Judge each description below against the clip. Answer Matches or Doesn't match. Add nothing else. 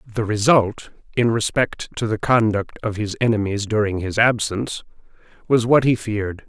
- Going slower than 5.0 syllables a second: Matches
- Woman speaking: Doesn't match